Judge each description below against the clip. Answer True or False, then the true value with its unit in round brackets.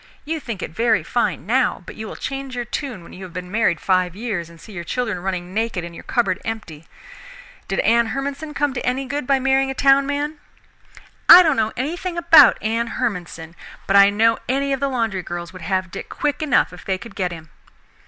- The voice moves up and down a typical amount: False (6.7 semitones)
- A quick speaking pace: True (220 wpm)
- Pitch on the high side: True (225 Hz)